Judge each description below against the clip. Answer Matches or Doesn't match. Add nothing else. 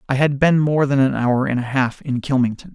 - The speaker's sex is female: Doesn't match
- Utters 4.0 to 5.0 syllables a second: Doesn't match